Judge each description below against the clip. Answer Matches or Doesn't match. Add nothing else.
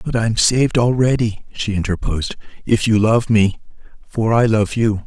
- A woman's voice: Doesn't match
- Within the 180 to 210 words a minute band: Doesn't match